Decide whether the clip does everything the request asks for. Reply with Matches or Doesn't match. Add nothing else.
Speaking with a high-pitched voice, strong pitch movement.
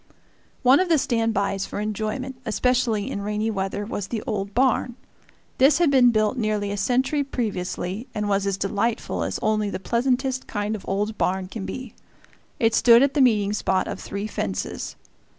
Doesn't match